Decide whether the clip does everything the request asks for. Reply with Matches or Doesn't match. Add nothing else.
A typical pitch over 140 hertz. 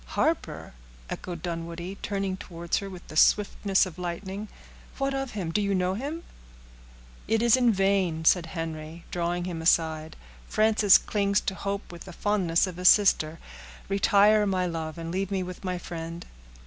Matches